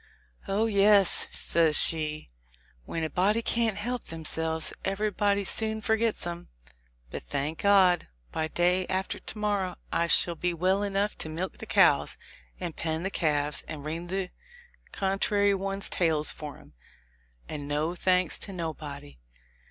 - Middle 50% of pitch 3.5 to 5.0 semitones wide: Yes, average, 4.0 semitones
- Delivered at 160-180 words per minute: No, average, 145 wpm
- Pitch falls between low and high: Yes, medium, 180 Hz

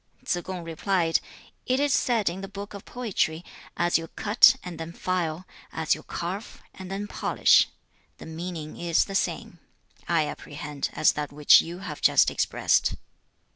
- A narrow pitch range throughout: No, average, 3.3 semitones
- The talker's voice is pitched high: No, medium, 175 Hz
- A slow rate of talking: No, average, 170 wpm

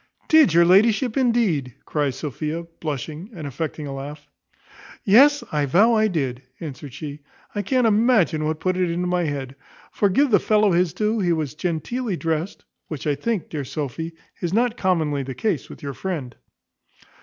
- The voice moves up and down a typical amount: No, wide, 6.2 semitones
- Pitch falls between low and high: Yes, medium, 170 Hz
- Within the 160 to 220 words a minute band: Yes, average, 175 wpm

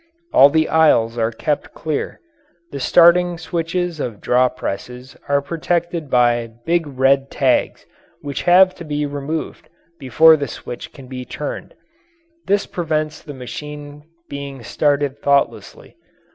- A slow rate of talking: Yes, slow, 130 wpm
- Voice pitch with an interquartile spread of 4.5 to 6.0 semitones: No, average, 3.5 semitones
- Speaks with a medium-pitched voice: Yes, medium, 145 Hz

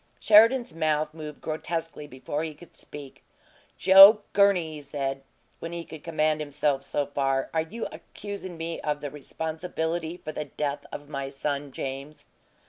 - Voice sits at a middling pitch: Yes, medium, 155 Hz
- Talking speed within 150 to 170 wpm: Yes, average, 155 wpm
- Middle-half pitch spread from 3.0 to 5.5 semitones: No, narrow, 2.5 semitones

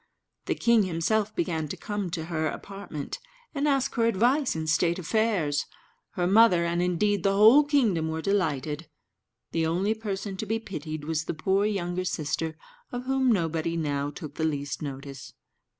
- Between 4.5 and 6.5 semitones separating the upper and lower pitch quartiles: Yes, average, 5.1 semitones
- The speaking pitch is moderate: Yes, medium, 175 Hz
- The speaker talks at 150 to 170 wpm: Yes, average, 165 wpm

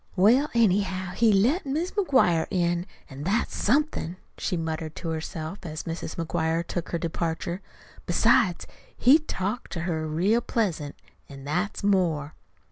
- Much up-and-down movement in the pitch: No, average, 4.8 semitones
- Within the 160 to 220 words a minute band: No, average, 140 wpm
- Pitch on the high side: No, medium, 180 Hz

